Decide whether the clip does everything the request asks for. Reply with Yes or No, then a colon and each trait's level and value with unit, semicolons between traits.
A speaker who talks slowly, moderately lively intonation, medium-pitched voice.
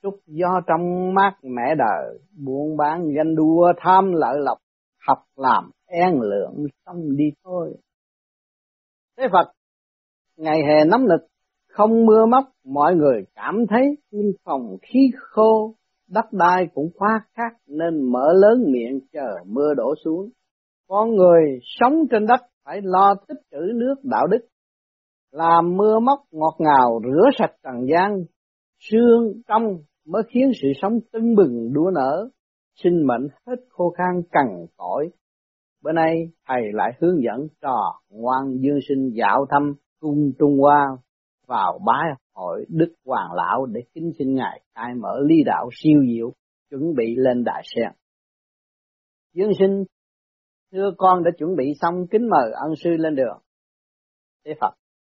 No: slow, 150 wpm; wide, 6.4 semitones; medium, 170 Hz